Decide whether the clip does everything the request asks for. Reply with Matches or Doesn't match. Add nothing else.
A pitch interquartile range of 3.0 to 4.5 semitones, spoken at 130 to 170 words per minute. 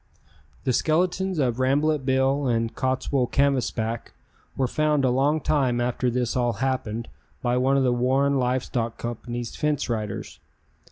Doesn't match